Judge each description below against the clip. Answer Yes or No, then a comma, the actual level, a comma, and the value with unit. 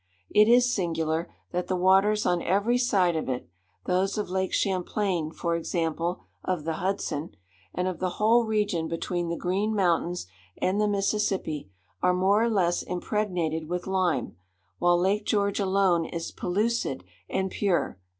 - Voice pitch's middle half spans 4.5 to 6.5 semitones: No, average, 3.2 semitones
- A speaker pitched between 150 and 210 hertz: Yes, medium, 185 Hz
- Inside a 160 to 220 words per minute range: No, average, 150 wpm